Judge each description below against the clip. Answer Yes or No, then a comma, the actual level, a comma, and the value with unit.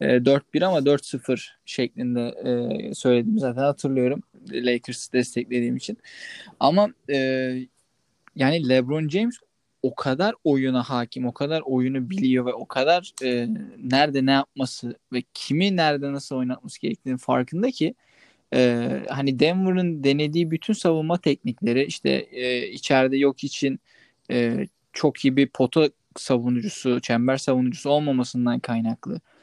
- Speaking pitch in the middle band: No, low, 130 Hz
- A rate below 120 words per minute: Yes, average, 110 wpm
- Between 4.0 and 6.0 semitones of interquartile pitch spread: No, average, 3.2 semitones